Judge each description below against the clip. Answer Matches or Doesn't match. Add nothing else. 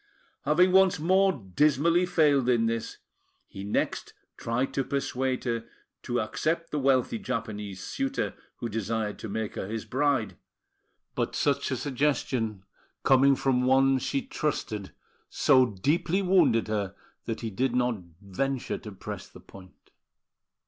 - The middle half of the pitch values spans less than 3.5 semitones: Doesn't match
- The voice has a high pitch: Doesn't match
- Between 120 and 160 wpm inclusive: Matches